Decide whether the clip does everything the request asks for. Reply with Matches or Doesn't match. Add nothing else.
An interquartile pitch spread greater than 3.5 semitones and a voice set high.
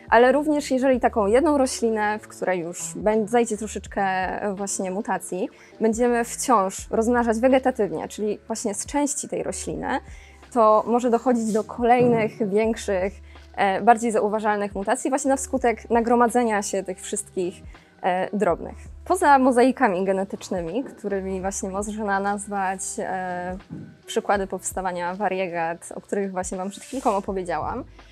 Matches